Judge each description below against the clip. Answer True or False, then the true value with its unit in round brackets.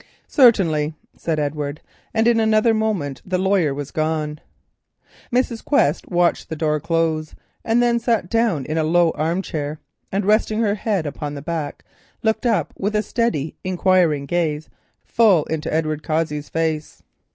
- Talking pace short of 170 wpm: True (150 wpm)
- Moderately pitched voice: True (165 Hz)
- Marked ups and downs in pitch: True (5.9 semitones)